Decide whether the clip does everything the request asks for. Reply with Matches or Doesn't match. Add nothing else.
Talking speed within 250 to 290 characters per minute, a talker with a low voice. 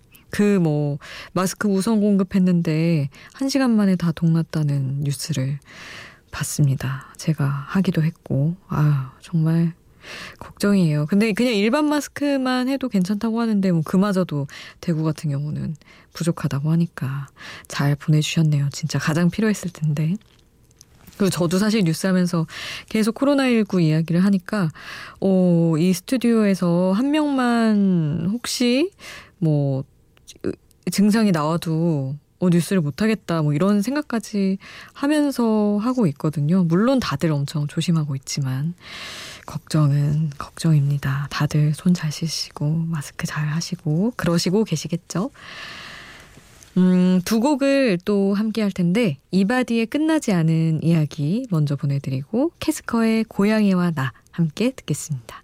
Doesn't match